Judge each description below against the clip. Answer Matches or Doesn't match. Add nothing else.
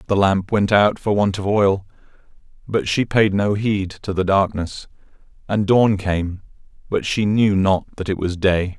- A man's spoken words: Matches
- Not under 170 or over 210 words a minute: Matches